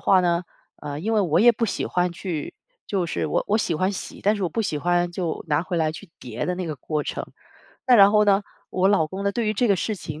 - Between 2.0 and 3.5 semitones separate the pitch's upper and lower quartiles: No, average, 4.2 semitones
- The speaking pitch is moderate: Yes, medium, 180 Hz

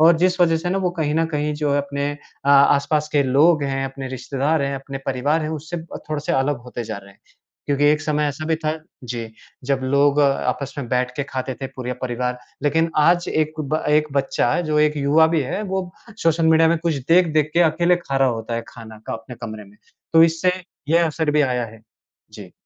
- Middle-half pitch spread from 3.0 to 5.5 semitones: Yes, average, 3.3 semitones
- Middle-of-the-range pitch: Yes, medium, 145 Hz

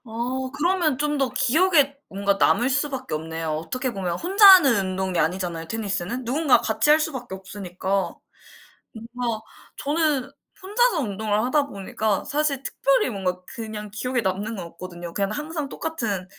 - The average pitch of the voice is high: Yes, high, 235 Hz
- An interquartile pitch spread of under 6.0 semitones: No, wide, 7.1 semitones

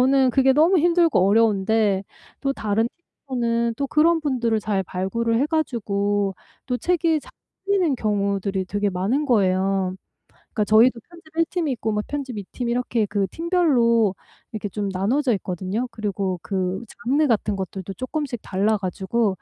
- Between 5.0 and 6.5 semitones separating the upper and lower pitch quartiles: Yes, wide, 5.5 semitones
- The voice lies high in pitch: Yes, high, 225 Hz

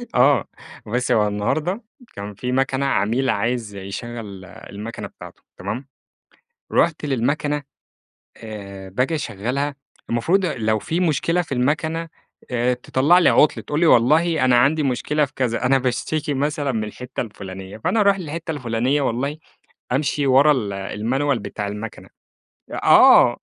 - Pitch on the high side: No, low, 130 Hz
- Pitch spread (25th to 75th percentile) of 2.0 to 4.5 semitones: No, average, 5.2 semitones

